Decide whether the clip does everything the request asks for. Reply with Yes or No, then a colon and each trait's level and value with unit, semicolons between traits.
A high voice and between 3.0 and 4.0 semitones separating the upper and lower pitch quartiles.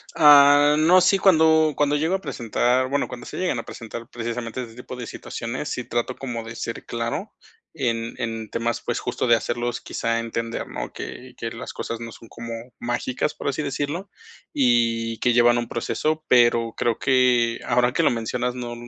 No: low, 120 Hz; average, 3.5 semitones